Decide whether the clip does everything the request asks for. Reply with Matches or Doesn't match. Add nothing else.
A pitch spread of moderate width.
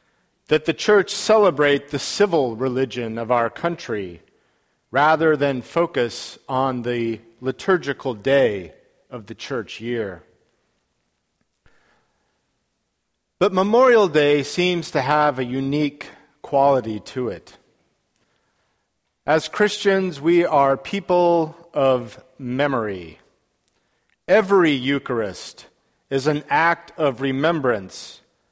Matches